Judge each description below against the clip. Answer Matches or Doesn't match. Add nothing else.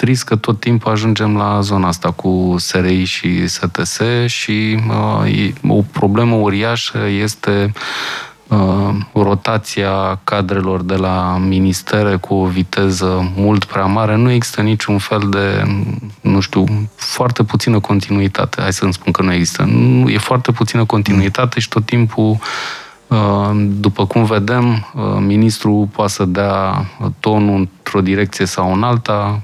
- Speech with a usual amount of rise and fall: Doesn't match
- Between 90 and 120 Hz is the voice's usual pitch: Matches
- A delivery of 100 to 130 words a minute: Doesn't match